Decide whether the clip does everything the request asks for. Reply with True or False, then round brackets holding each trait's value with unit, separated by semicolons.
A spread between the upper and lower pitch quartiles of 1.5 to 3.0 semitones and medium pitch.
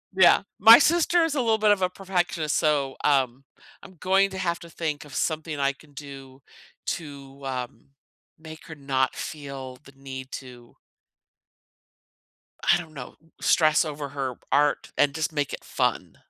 False (4.3 semitones; 150 Hz)